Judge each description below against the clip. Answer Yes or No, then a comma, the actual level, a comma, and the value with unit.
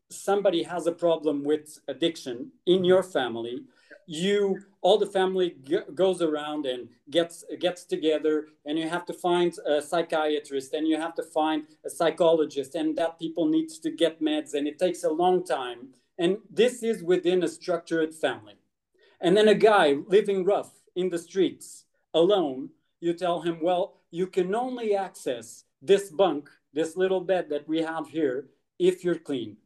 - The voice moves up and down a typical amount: Yes, average, 3.3 semitones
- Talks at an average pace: Yes, average, 170 wpm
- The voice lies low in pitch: No, medium, 170 Hz